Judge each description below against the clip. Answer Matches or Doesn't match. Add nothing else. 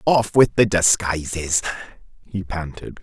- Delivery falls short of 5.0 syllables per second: Matches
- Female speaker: Doesn't match